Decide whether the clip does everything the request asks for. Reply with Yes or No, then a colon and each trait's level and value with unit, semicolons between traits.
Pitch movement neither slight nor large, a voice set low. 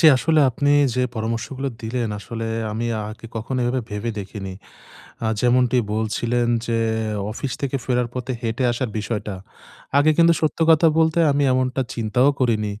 Yes: average, 3.1 semitones; low, 120 Hz